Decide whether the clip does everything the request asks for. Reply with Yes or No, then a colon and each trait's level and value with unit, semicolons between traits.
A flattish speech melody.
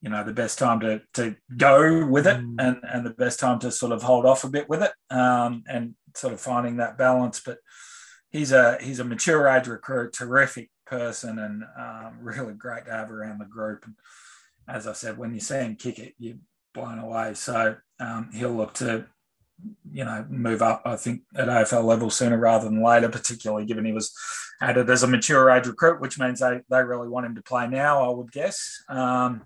Yes: narrow, 2.2 semitones